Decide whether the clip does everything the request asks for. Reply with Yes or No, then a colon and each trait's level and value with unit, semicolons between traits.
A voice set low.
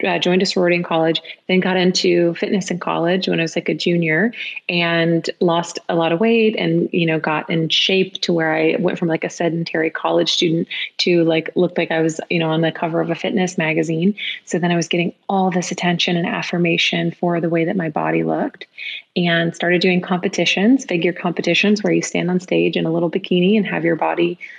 No: medium, 175 Hz